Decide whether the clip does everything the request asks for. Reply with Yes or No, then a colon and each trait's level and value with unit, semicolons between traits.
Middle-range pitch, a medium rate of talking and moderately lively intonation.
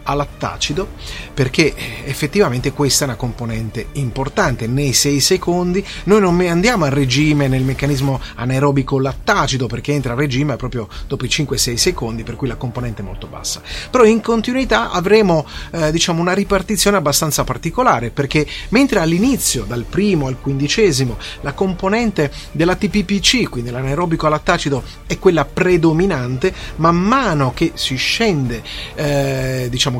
No: medium, 145 Hz; average, 140 wpm; wide, 5.9 semitones